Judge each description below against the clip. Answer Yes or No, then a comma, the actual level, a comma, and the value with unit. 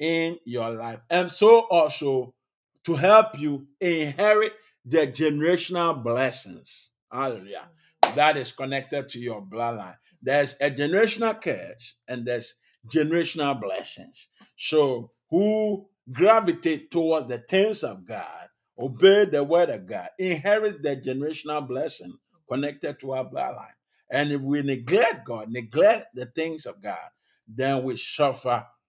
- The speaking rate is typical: No, slow, 130 wpm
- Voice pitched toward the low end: No, medium, 145 Hz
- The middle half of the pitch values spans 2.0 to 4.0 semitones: No, average, 5.1 semitones